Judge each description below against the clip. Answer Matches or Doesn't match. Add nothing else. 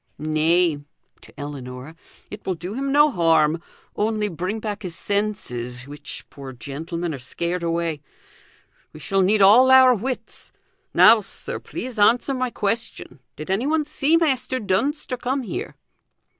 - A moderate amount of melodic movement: Doesn't match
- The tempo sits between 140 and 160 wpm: Matches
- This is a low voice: Doesn't match